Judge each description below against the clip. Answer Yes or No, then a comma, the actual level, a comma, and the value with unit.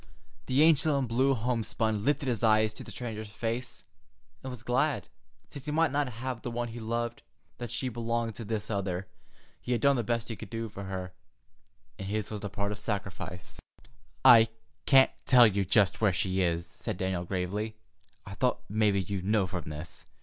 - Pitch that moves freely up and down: No, average, 3.5 semitones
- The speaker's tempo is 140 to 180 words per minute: No, average, 195 wpm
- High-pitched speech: No, low, 110 Hz